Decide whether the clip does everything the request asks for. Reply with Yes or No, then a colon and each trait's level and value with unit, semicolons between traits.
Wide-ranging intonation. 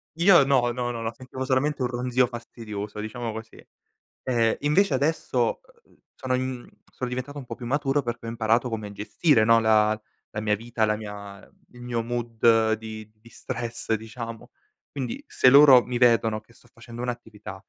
No: narrow, 2.5 semitones